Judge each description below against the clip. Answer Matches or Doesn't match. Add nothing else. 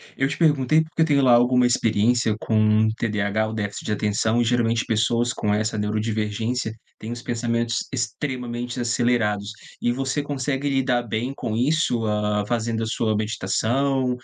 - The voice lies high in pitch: Doesn't match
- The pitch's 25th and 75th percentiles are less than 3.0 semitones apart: Matches